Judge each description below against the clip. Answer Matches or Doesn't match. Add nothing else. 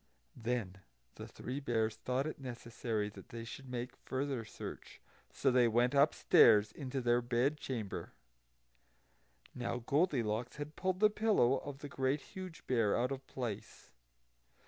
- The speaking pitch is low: Matches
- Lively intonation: Doesn't match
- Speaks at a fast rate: Doesn't match